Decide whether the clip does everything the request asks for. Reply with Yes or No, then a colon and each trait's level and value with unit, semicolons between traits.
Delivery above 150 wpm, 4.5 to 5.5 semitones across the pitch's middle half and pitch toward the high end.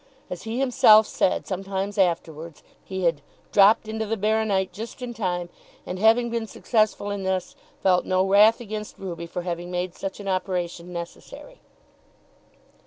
No: average, 160 wpm; average, 3.4 semitones; high, 195 Hz